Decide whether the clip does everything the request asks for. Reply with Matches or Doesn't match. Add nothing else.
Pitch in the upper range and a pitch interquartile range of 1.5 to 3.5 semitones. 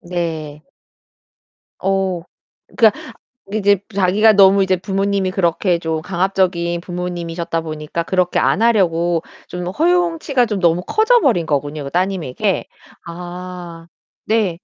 Doesn't match